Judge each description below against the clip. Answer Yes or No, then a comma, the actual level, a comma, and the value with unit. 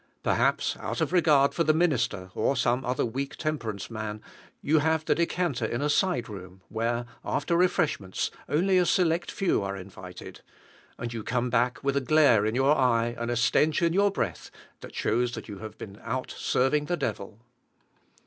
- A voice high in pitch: No, low, 125 Hz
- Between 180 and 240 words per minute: Yes, average, 185 wpm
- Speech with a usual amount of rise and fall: No, wide, 5.9 semitones